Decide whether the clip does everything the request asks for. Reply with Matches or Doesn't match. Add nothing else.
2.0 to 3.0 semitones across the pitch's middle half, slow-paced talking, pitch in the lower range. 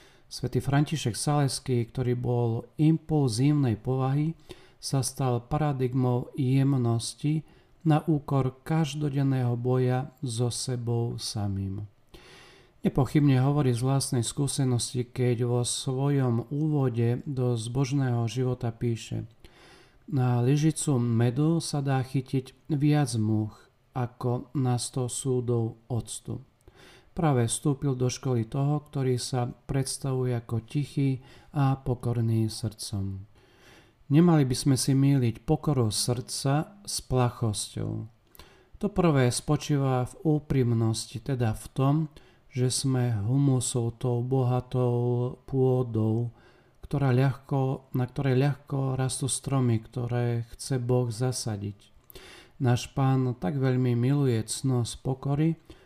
Matches